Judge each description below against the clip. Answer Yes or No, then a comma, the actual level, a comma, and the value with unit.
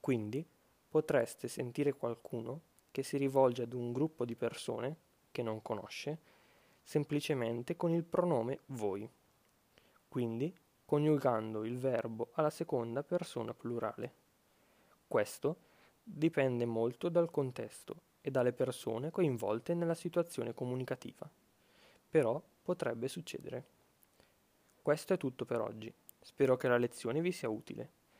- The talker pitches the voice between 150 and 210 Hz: No, low, 135 Hz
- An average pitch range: Yes, average, 4.7 semitones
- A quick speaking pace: No, slow, 115 wpm